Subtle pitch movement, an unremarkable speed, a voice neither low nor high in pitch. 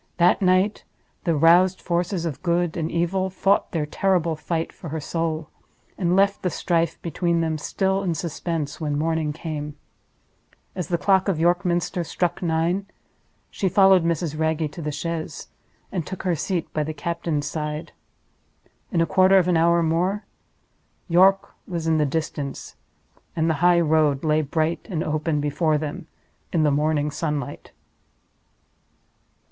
Yes: narrow, 2.3 semitones; average, 150 wpm; medium, 165 Hz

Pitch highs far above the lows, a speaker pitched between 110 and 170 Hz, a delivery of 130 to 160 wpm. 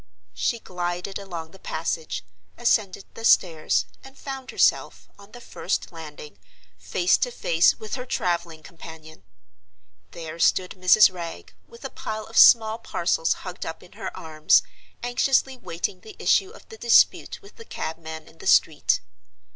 No: wide, 5.9 semitones; medium, 180 Hz; average, 155 wpm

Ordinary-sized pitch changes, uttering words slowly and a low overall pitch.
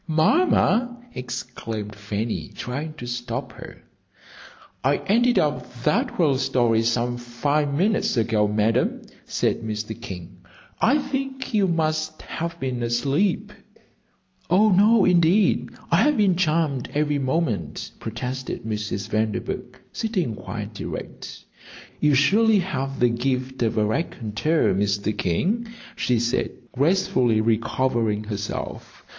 No: wide, 6.9 semitones; slow, 115 wpm; low, 130 Hz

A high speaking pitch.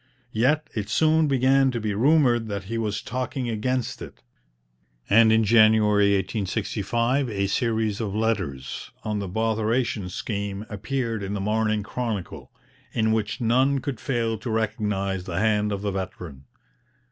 No: low, 110 Hz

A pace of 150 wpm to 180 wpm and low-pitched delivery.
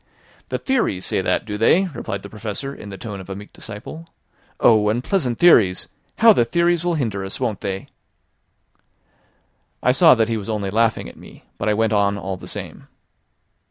No: average, 190 wpm; low, 110 Hz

